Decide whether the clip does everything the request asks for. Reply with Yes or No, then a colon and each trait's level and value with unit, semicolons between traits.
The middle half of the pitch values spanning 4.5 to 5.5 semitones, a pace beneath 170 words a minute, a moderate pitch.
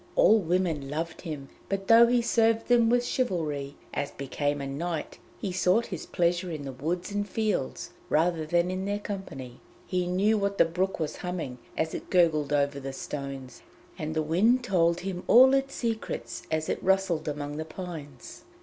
No: average, 5.1 semitones; average, 180 wpm; medium, 175 Hz